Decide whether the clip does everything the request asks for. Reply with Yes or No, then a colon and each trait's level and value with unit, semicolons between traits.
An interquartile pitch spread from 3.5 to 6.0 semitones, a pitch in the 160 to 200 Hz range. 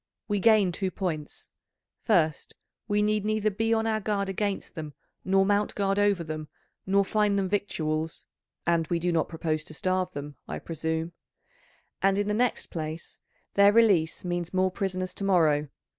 Yes: average, 4.1 semitones; medium, 185 Hz